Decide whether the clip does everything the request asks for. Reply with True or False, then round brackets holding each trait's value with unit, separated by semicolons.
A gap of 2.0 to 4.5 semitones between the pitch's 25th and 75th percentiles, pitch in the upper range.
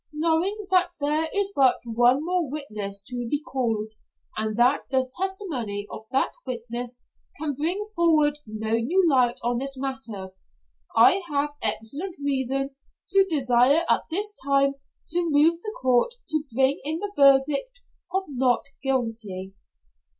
False (5.0 semitones; 275 Hz)